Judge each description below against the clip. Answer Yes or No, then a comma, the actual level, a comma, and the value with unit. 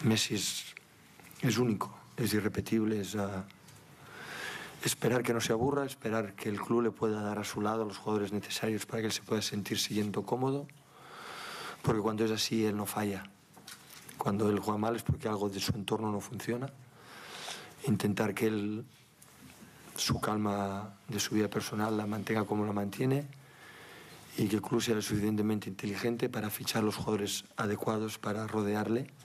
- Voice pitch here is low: Yes, low, 110 Hz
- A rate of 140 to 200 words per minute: Yes, average, 170 wpm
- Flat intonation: Yes, narrow, 1.7 semitones